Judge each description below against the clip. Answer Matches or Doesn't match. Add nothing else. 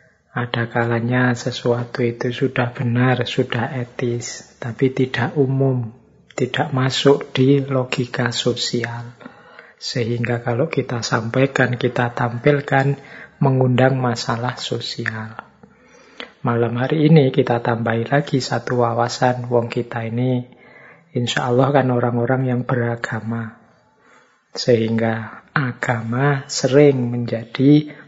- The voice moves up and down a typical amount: Doesn't match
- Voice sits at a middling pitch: Doesn't match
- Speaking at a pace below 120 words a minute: Matches